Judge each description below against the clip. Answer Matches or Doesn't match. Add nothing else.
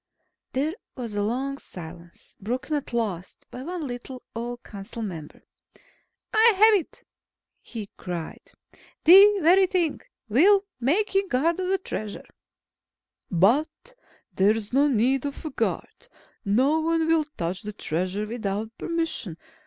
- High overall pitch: Matches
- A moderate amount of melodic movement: Doesn't match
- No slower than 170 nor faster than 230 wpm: Doesn't match